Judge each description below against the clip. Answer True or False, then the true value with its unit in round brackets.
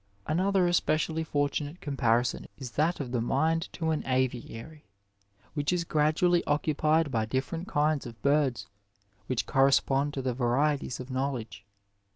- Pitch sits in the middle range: True (145 Hz)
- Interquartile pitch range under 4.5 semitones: True (3.6 semitones)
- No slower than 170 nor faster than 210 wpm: False (145 wpm)